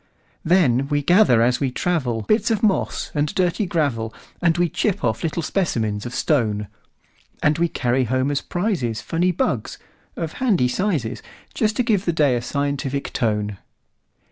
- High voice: No, medium, 145 Hz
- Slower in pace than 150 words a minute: Yes, average, 140 wpm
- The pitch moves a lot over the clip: Yes, wide, 6.6 semitones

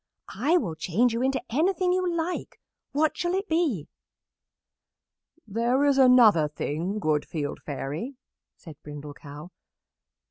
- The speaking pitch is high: Yes, high, 235 Hz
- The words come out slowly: Yes, slow, 130 wpm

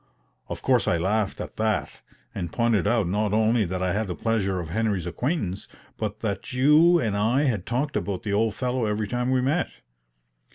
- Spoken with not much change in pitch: No, average, 3.8 semitones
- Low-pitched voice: Yes, low, 110 Hz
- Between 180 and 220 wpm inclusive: Yes, average, 195 wpm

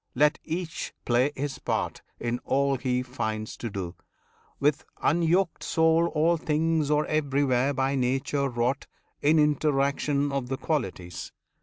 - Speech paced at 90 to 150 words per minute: Yes, slow, 135 wpm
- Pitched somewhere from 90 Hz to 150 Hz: Yes, medium, 140 Hz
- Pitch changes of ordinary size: Yes, average, 3.3 semitones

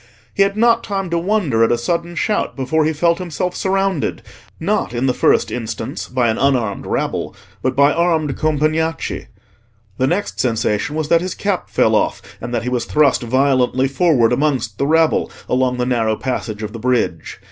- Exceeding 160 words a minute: Yes, average, 185 wpm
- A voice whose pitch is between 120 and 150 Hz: Yes, medium, 140 Hz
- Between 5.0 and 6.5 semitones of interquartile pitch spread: Yes, wide, 5.6 semitones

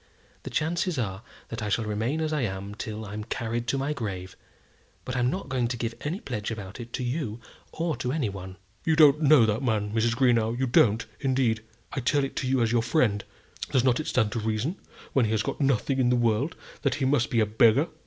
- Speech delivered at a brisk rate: Yes, fast, 230 wpm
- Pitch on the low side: Yes, low, 120 Hz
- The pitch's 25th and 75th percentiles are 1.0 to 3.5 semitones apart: No, average, 3.9 semitones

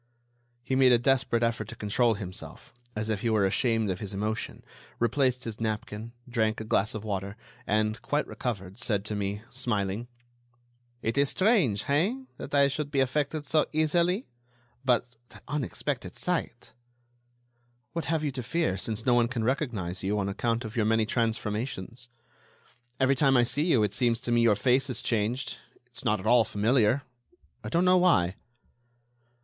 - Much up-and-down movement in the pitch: No, average, 4.0 semitones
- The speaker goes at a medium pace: Yes, average, 175 wpm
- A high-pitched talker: No, low, 120 Hz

